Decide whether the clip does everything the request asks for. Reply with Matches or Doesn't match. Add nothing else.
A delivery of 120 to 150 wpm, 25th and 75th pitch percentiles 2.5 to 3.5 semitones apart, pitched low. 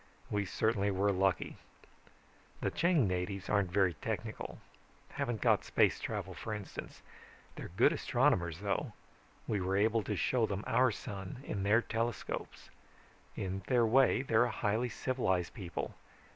Matches